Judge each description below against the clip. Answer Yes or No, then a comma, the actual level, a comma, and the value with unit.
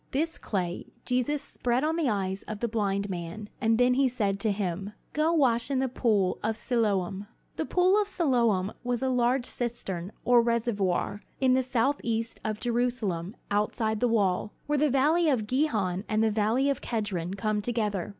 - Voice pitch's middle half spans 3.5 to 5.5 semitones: Yes, average, 4.0 semitones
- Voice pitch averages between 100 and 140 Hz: No, high, 230 Hz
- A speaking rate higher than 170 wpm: Yes, average, 180 wpm